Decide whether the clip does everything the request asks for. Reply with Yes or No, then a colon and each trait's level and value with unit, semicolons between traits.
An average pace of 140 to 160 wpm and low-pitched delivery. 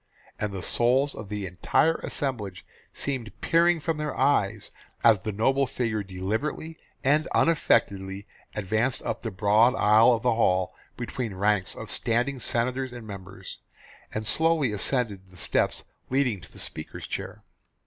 Yes: average, 150 wpm; low, 115 Hz